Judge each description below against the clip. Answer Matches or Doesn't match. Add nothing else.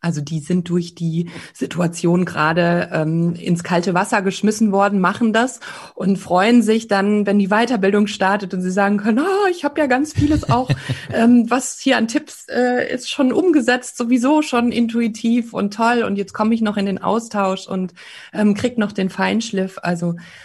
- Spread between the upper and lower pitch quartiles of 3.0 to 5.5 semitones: Matches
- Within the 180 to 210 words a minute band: Matches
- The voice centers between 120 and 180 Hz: Doesn't match